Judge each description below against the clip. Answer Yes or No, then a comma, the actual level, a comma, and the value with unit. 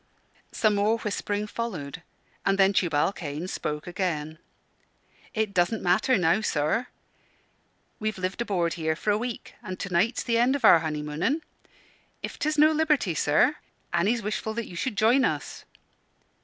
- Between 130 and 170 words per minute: Yes, average, 155 wpm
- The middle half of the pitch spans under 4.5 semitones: No, average, 5.3 semitones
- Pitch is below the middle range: No, high, 200 Hz